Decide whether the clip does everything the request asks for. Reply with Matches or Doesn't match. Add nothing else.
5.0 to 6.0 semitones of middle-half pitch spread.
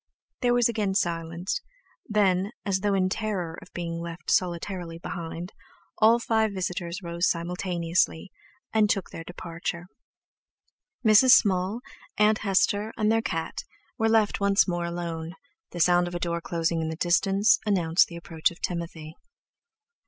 Doesn't match